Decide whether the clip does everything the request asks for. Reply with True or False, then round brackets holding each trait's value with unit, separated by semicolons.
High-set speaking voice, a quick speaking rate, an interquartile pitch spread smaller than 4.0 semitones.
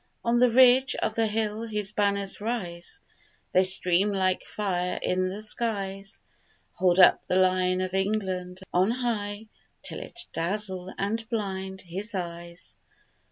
False (195 Hz; 140 wpm; 2.8 semitones)